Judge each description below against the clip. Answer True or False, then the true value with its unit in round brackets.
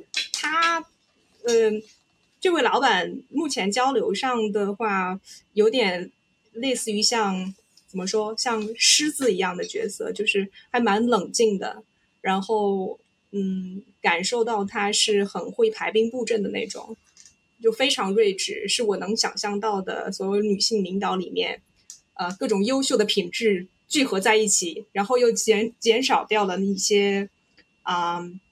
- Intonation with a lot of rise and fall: False (3.3 semitones)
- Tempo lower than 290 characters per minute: True (210 characters per minute)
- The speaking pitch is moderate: False (215 Hz)